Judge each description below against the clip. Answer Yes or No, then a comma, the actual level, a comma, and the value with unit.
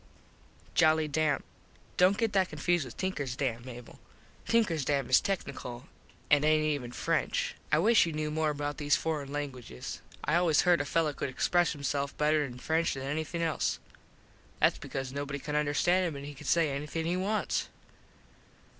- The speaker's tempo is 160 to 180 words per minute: Yes, average, 170 wpm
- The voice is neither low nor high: Yes, medium, 150 Hz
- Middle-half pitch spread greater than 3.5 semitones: No, average, 2.9 semitones